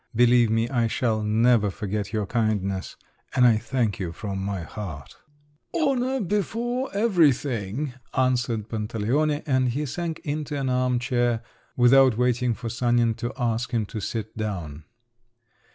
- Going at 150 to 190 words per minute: No, average, 140 wpm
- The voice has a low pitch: Yes, low, 120 Hz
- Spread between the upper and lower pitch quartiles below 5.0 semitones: Yes, average, 3.7 semitones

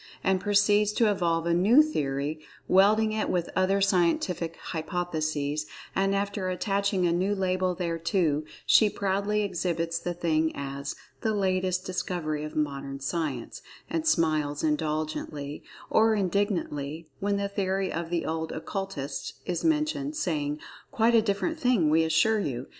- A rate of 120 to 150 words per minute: Yes, average, 140 wpm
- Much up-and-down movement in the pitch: No, average, 4.3 semitones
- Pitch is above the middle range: No, medium, 180 Hz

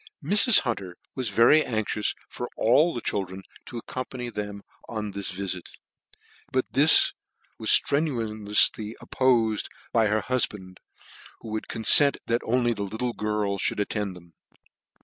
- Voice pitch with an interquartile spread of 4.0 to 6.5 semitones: No, average, 3.3 semitones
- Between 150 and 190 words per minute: No, slow, 135 wpm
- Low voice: Yes, low, 110 Hz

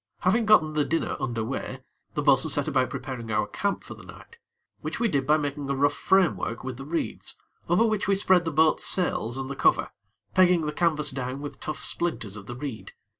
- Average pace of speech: No, fast, 215 wpm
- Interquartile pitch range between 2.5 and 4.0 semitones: No, average, 4.8 semitones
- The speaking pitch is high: No, medium, 145 Hz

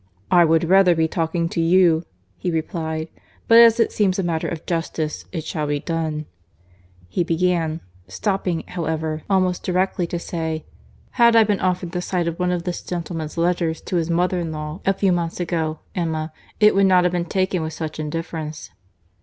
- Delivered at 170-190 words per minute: Yes, average, 185 wpm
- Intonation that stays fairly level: Yes, narrow, 2.2 semitones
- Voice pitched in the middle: Yes, medium, 170 Hz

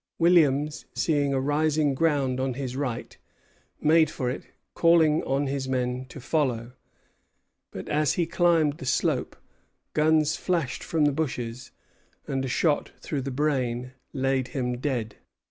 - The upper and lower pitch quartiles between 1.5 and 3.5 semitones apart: Yes, average, 3.1 semitones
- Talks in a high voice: No, medium, 140 Hz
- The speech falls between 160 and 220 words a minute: No, average, 145 wpm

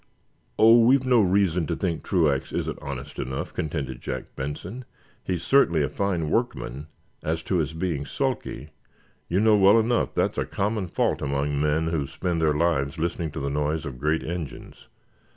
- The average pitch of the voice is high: No, very low, 80 Hz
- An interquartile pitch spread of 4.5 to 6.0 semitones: Yes, average, 4.8 semitones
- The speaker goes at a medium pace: Yes, average, 170 wpm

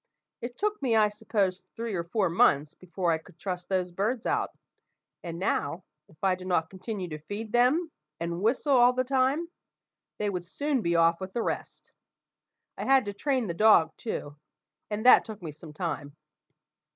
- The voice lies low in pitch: No, high, 195 Hz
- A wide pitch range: Yes, wide, 6.0 semitones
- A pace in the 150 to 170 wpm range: No, average, 185 wpm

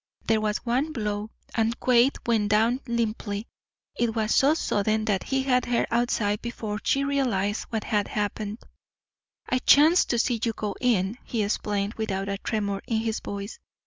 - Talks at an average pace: Yes, average, 170 wpm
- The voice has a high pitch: Yes, high, 220 Hz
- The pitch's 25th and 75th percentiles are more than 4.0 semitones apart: No, average, 2.7 semitones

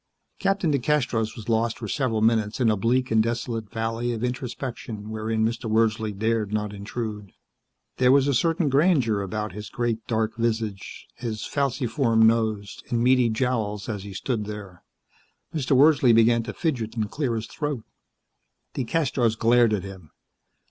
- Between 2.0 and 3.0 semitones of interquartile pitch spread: Yes, narrow, 2.6 semitones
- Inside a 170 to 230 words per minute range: No, average, 155 wpm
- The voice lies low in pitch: Yes, low, 115 Hz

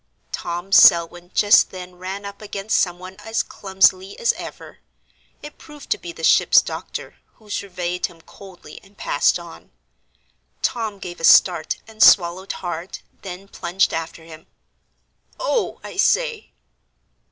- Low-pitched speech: No, high, 190 Hz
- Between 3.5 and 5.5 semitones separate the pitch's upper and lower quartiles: No, average, 3.1 semitones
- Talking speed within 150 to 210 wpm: No, average, 140 wpm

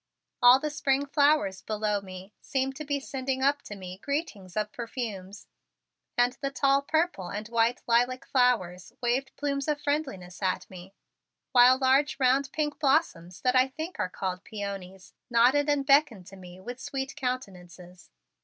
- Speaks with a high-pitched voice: Yes, very high, 250 Hz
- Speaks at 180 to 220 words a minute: No, average, 160 wpm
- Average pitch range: No, wide, 6.2 semitones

